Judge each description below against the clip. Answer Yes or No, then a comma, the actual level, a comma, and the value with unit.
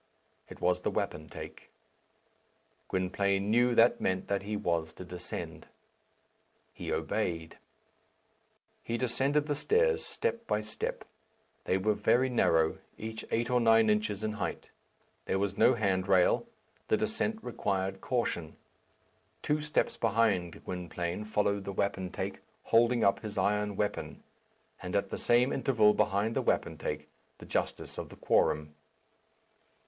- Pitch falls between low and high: No, low, 105 Hz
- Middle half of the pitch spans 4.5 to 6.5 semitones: No, average, 4.0 semitones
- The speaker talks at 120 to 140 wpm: Yes, slow, 135 wpm